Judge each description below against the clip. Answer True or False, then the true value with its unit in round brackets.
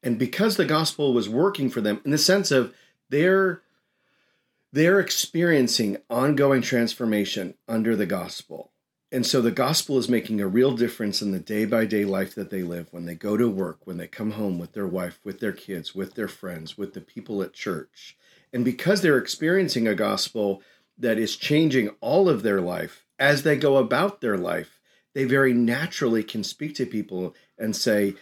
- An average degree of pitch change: False (6.0 semitones)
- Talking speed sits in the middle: True (190 wpm)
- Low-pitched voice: True (120 Hz)